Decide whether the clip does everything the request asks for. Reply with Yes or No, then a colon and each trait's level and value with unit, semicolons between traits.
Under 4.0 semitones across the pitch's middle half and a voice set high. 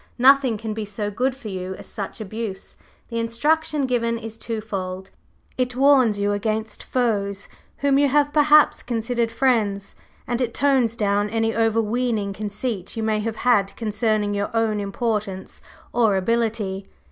Yes: average, 3.1 semitones; high, 225 Hz